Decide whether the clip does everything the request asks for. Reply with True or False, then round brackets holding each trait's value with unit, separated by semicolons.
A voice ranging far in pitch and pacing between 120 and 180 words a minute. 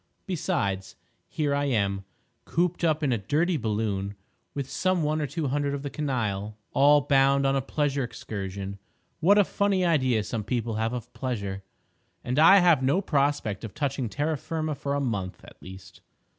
True (5.7 semitones; 175 wpm)